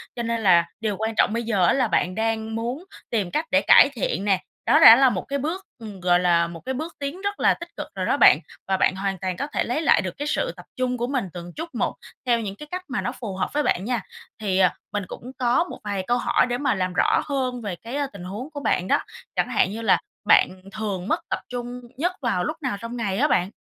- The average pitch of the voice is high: Yes, high, 230 Hz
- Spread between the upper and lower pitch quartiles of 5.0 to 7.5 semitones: Yes, wide, 5.4 semitones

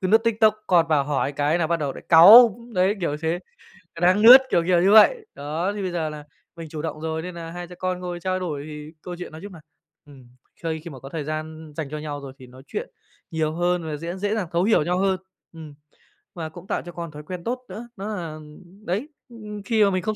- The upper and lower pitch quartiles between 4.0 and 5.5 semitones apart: No, average, 3.6 semitones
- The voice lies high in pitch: No, medium, 170 Hz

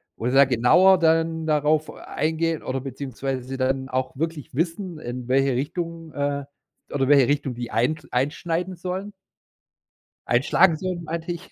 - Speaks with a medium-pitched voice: Yes, medium, 145 Hz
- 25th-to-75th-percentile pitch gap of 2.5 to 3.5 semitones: No, average, 4.0 semitones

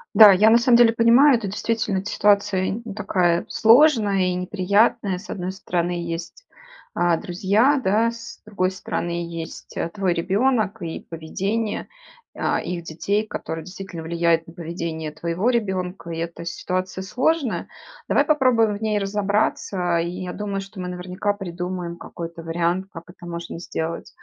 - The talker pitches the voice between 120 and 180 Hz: No, high, 190 Hz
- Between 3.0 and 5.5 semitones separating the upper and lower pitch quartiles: Yes, average, 3.8 semitones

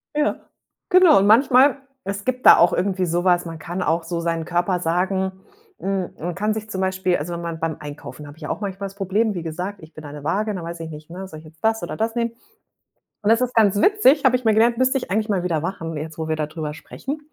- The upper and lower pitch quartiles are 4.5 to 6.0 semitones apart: Yes, average, 4.8 semitones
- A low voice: No, medium, 185 Hz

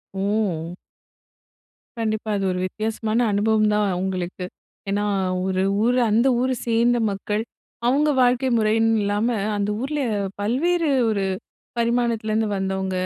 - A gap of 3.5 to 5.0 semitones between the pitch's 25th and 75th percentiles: No, average, 2.9 semitones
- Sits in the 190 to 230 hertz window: Yes, high, 215 Hz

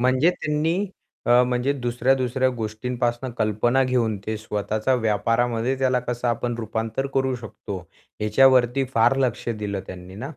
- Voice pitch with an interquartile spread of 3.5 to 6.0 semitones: No, average, 2.8 semitones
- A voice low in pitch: Yes, low, 120 Hz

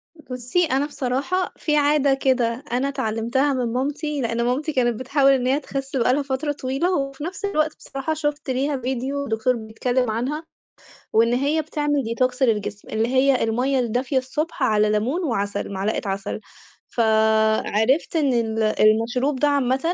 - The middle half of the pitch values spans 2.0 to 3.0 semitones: No, average, 3.8 semitones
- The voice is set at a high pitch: Yes, very high, 260 Hz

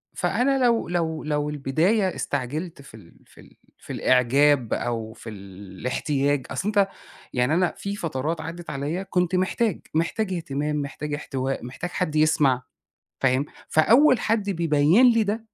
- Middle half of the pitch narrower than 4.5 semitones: No, wide, 5.5 semitones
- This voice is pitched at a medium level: Yes, medium, 155 Hz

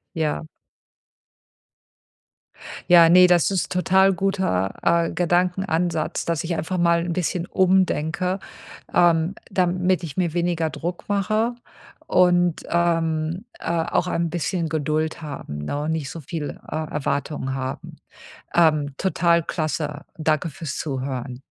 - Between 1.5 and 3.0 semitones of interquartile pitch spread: Yes, narrow, 2.6 semitones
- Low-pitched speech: No, medium, 170 Hz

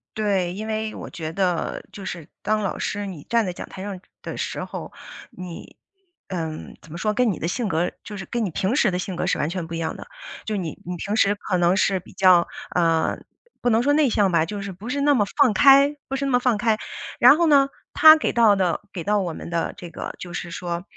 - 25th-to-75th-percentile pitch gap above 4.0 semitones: Yes, average, 4.4 semitones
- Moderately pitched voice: No, high, 195 Hz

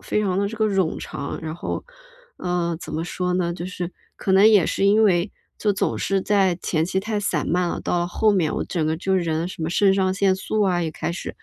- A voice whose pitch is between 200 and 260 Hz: No, medium, 185 Hz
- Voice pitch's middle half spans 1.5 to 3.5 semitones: Yes, narrow, 2.6 semitones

